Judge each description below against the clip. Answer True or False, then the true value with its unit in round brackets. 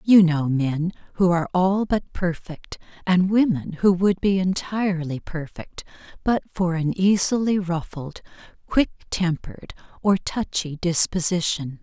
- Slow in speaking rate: True (125 wpm)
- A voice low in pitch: False (175 Hz)